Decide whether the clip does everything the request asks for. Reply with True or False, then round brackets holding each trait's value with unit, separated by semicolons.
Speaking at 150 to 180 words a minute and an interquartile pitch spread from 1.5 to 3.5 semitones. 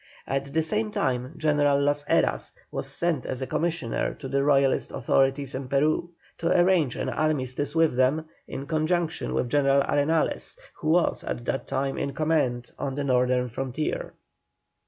True (160 wpm; 3.1 semitones)